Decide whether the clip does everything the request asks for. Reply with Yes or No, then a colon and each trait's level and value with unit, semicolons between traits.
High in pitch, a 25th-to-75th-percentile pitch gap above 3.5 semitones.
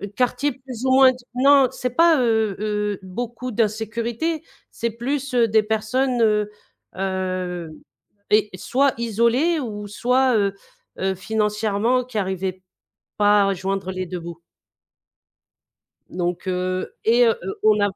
Yes: high, 220 Hz; average, 4.3 semitones